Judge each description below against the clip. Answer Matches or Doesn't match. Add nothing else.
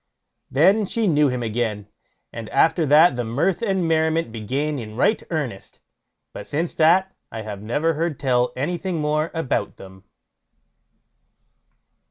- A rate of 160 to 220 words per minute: Doesn't match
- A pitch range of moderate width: Doesn't match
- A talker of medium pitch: Matches